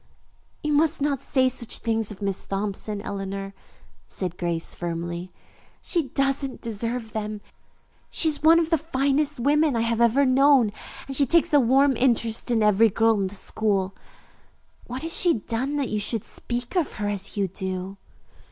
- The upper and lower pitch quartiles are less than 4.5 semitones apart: No, wide, 5.5 semitones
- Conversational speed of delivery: Yes, average, 170 wpm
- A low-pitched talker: No, high, 230 Hz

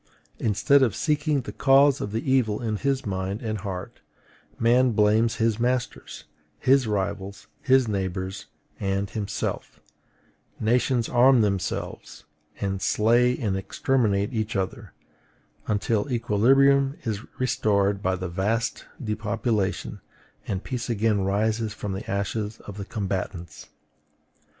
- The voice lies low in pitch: Yes, low, 110 Hz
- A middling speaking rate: No, slow, 120 wpm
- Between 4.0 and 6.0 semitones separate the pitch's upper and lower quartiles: No, average, 3.6 semitones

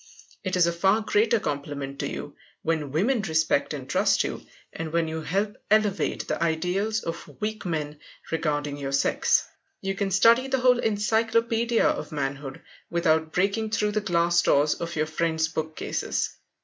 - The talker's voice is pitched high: No, medium, 170 Hz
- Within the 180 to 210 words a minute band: No, average, 160 wpm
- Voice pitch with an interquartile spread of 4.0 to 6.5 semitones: Yes, average, 5.2 semitones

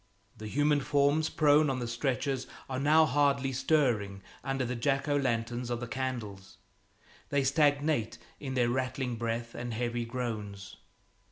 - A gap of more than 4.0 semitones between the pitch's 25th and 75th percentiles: No, average, 3.2 semitones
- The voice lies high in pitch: No, low, 130 Hz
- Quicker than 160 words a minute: No, average, 150 wpm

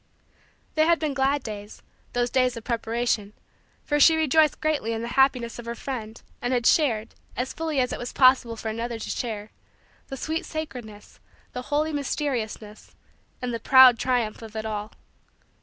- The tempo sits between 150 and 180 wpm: Yes, average, 175 wpm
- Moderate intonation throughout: Yes, average, 3.8 semitones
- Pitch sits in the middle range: No, high, 245 Hz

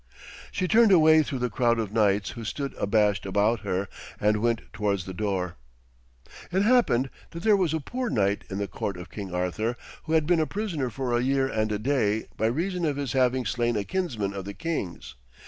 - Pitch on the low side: Yes, low, 120 Hz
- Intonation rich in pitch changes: Yes, wide, 7.4 semitones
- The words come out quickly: Yes, fast, 210 wpm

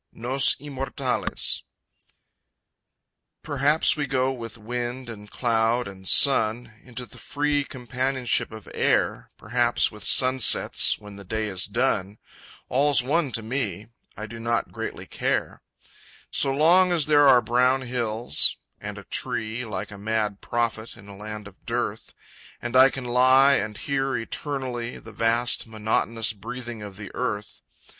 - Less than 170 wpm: Yes, average, 145 wpm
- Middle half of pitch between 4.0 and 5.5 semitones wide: No, average, 3.3 semitones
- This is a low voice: Yes, low, 120 Hz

